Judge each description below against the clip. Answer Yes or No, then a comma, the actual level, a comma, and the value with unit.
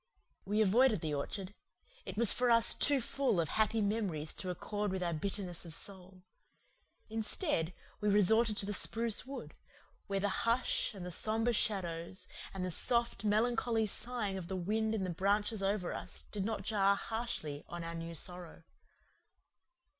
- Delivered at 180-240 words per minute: No, average, 165 wpm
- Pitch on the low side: No, high, 205 Hz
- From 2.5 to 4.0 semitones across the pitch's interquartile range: Yes, average, 3.6 semitones